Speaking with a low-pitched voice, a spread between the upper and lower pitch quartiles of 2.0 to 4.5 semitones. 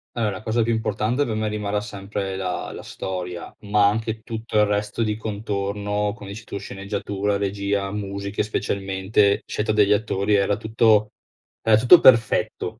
No: low, 105 Hz; narrow, 1.6 semitones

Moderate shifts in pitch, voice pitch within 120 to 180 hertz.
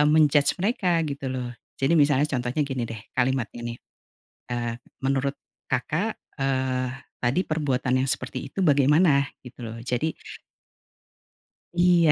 Yes: average, 3.1 semitones; low, 135 Hz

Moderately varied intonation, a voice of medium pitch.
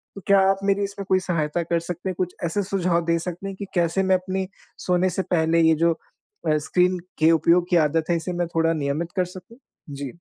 No: narrow, 2.3 semitones; medium, 175 Hz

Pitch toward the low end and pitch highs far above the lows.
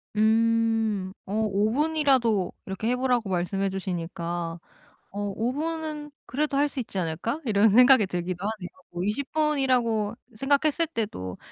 No: high, 225 Hz; wide, 5.8 semitones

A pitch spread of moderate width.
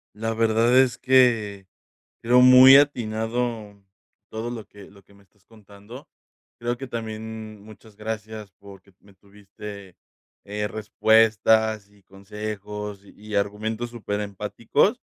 No: narrow, 1.9 semitones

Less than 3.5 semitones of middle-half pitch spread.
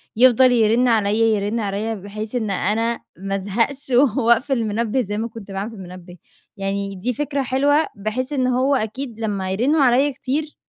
No: average, 4.0 semitones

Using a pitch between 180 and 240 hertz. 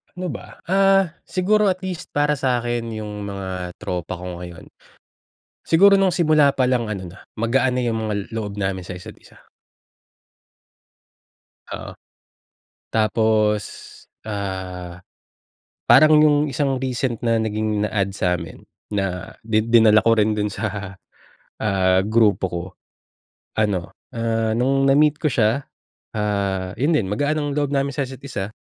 No: low, 110 Hz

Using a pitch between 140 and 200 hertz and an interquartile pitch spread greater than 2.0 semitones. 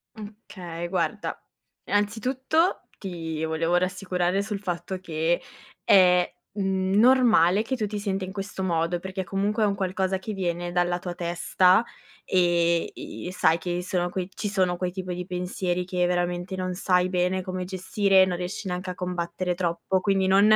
No: medium, 185 Hz; narrow, 1.7 semitones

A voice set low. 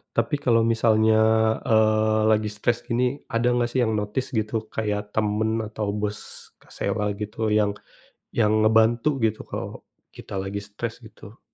Yes: low, 110 Hz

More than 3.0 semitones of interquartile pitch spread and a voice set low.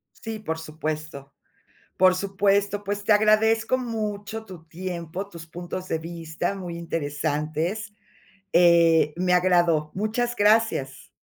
No: average, 4.2 semitones; medium, 180 Hz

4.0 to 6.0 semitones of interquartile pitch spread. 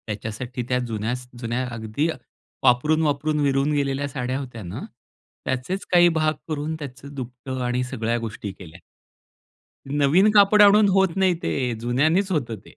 Yes: average, 4.3 semitones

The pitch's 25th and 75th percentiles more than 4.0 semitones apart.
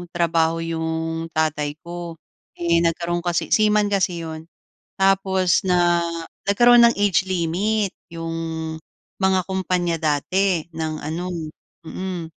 No: narrow, 2.5 semitones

